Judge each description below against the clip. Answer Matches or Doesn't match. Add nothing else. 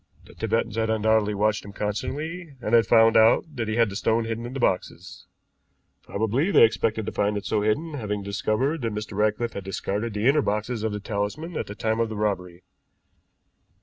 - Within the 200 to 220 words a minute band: Matches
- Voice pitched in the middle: Doesn't match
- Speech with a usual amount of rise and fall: Doesn't match